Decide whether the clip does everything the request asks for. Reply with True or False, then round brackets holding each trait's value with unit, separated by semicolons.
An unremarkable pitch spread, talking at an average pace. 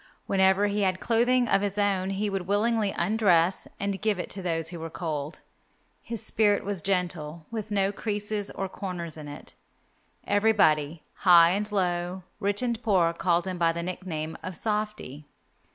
True (3.3 semitones; 170 wpm)